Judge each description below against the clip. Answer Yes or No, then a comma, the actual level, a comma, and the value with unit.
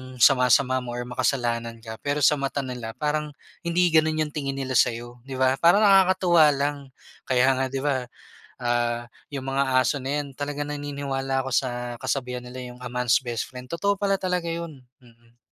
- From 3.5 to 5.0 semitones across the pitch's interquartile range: No, average, 3.1 semitones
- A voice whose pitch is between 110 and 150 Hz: Yes, low, 135 Hz